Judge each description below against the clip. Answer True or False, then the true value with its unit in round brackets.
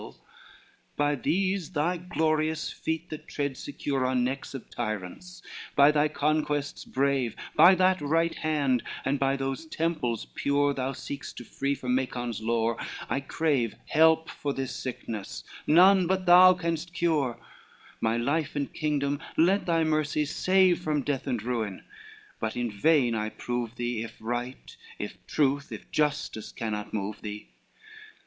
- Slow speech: False (150 wpm)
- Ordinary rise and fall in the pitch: True (4.6 semitones)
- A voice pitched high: False (140 Hz)